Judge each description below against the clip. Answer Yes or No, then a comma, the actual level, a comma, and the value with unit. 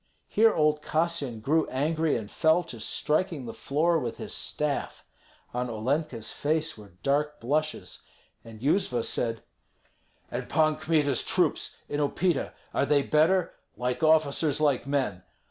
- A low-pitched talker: No, medium, 150 Hz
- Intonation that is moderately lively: Yes, average, 4.1 semitones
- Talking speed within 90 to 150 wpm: Yes, average, 140 wpm